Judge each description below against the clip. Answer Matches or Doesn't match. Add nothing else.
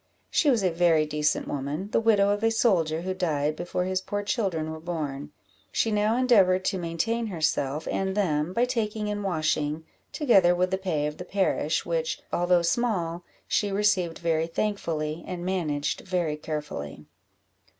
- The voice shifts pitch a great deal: Doesn't match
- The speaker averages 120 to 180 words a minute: Matches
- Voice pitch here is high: Doesn't match